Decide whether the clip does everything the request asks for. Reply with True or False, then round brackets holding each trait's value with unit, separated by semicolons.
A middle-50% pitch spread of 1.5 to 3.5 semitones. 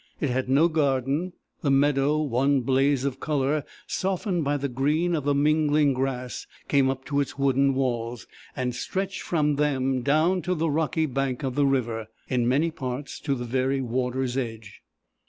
True (2.5 semitones)